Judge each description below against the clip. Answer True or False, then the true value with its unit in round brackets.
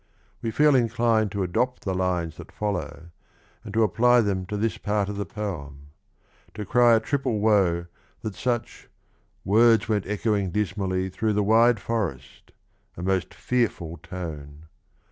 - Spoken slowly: False (155 wpm)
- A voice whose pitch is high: False (105 Hz)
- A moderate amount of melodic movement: True (3.6 semitones)